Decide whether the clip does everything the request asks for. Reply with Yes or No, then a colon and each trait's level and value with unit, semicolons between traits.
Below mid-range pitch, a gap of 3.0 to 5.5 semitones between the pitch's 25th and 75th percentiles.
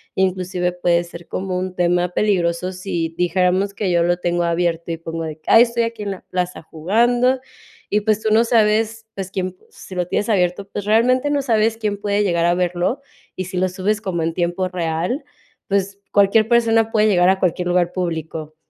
No: medium, 185 Hz; average, 3.4 semitones